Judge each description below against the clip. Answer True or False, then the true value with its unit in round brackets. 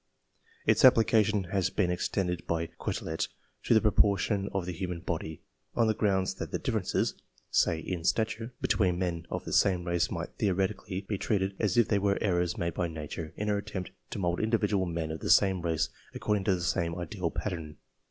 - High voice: False (95 Hz)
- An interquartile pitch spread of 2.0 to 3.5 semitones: True (3.2 semitones)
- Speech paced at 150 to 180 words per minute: False (190 wpm)